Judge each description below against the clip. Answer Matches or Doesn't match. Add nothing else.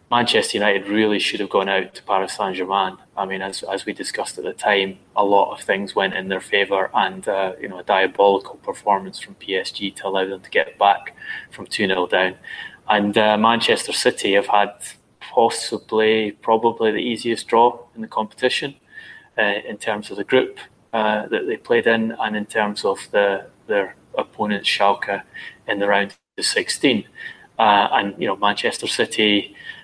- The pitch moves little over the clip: Matches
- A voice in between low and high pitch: Doesn't match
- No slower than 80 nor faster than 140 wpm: Doesn't match